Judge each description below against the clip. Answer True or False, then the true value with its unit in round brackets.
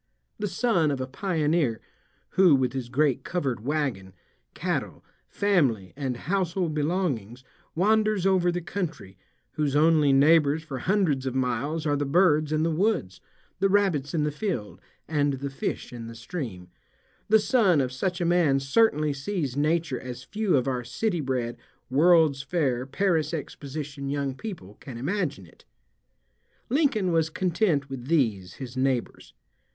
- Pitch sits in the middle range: True (150 Hz)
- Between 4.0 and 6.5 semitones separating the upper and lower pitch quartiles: True (5.2 semitones)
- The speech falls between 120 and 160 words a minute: True (150 wpm)